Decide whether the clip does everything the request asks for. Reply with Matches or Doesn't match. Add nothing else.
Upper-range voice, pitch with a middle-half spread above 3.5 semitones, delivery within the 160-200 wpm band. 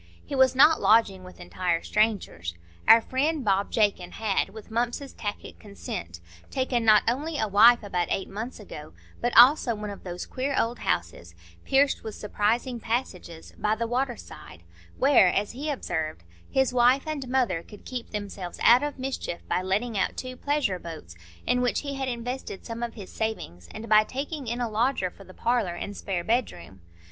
Matches